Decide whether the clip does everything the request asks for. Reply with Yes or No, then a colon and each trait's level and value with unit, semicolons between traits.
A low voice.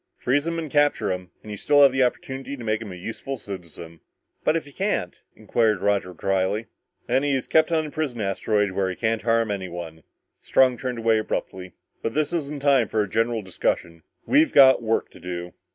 Yes: low, 115 Hz